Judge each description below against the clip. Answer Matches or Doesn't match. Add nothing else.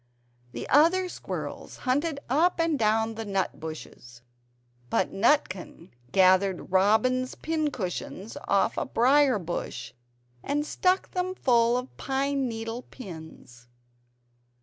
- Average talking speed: Doesn't match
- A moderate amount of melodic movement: Doesn't match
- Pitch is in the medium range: Doesn't match